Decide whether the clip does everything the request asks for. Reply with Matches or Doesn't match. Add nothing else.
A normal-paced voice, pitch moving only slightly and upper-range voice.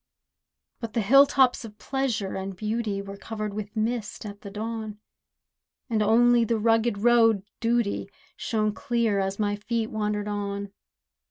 Matches